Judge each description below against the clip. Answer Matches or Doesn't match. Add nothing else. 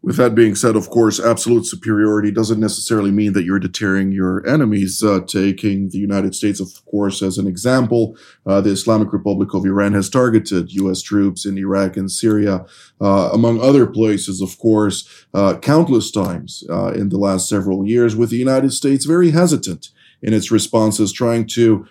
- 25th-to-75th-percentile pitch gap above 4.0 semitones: Doesn't match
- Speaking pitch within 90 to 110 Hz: Matches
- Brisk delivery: Doesn't match